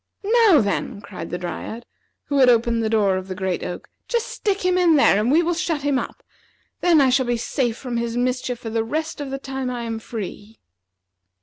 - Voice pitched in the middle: No, high, 245 Hz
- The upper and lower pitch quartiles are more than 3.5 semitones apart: Yes, average, 4.7 semitones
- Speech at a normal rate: No, fast, 220 wpm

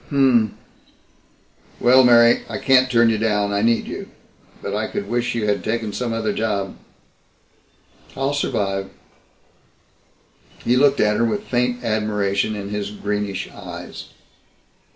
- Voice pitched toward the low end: Yes, low, 110 Hz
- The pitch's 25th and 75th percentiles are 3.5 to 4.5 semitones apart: No, average, 2.8 semitones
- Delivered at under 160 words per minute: Yes, average, 145 wpm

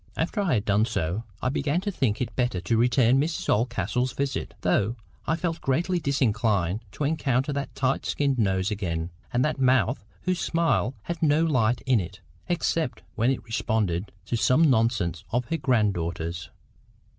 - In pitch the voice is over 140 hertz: No, low, 125 Hz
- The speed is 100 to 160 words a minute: No, average, 170 wpm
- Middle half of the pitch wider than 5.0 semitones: Yes, wide, 5.4 semitones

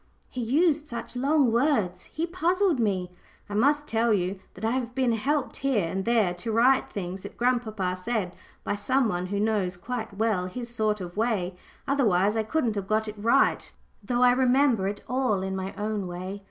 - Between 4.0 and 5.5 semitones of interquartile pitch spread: Yes, average, 4.7 semitones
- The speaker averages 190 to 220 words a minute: Yes, average, 195 wpm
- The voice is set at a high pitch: Yes, high, 220 Hz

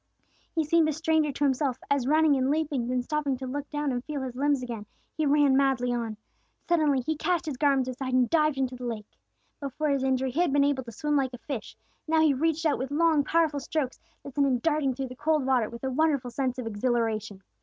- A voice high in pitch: Yes, very high, 275 Hz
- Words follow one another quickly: Yes, fast, 235 wpm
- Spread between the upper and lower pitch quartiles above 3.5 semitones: No, average, 3.1 semitones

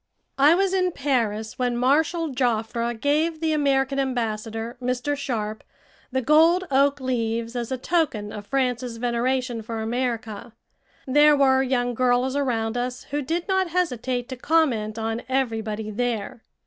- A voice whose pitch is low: No, very high, 250 Hz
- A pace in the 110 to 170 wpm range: Yes, average, 145 wpm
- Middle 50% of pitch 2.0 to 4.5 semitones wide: Yes, average, 3.8 semitones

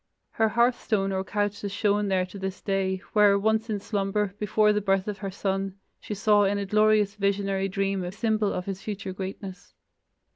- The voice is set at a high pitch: Yes, high, 200 Hz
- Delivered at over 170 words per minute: Yes, average, 195 wpm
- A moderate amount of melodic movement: No, narrow, 1.4 semitones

